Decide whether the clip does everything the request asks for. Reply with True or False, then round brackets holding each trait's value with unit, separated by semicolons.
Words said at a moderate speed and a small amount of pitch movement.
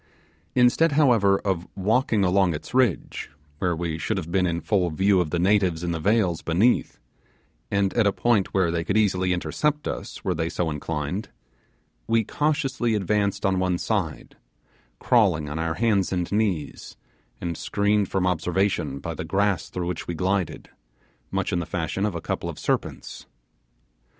False (170 wpm; 3.6 semitones)